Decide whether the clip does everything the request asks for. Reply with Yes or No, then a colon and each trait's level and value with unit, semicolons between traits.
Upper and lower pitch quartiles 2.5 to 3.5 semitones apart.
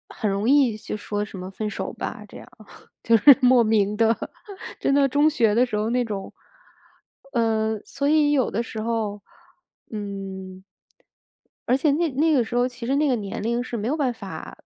No: average, 4.0 semitones